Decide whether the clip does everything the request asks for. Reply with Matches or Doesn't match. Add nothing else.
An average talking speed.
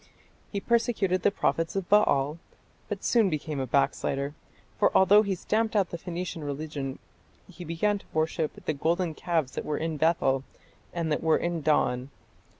Matches